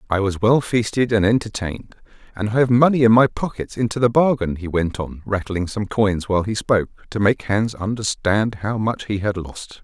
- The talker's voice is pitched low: Yes, low, 105 Hz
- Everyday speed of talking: No, fast, 210 wpm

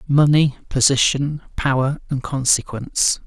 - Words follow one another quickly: No, slow, 90 wpm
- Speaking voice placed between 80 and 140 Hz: Yes, low, 135 Hz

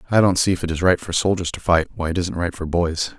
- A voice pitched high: No, very low, 90 Hz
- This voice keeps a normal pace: No, fast, 320 wpm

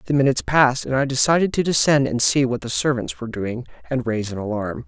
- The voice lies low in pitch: Yes, low, 125 Hz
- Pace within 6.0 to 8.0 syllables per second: Yes, 6.5 syllables/s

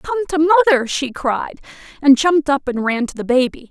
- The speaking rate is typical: No, fast, 210 wpm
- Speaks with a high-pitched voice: Yes, very high, 285 Hz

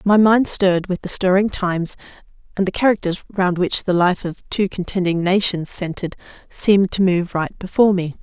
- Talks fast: No, average, 180 wpm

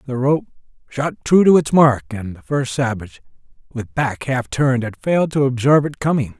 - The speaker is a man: Yes, male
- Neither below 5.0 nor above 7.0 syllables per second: Yes, 5.4 syllables/s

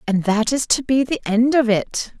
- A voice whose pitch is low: No, high, 235 Hz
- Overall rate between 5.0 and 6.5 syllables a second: No, 4.6 syllables/s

